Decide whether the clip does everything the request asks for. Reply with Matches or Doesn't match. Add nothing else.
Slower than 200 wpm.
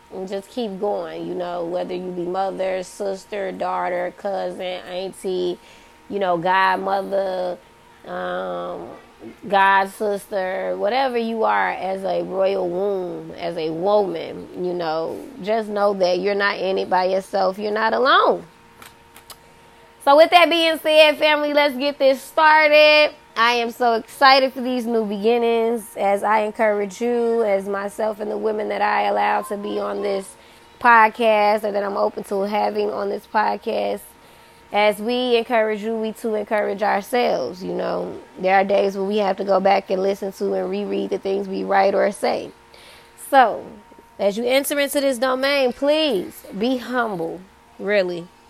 Matches